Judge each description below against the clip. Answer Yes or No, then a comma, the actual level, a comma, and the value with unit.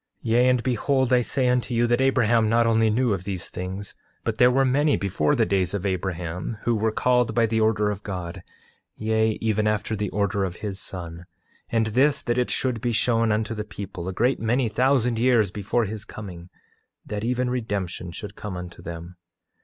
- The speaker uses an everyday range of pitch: Yes, average, 3.6 semitones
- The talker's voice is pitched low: Yes, low, 110 Hz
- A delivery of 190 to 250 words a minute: Yes, average, 200 wpm